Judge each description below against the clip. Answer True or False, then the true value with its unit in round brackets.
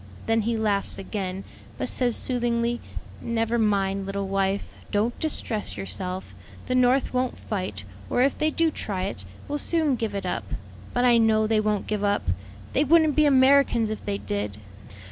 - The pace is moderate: True (170 wpm)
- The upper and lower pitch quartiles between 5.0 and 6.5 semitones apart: False (4.3 semitones)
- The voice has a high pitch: True (220 Hz)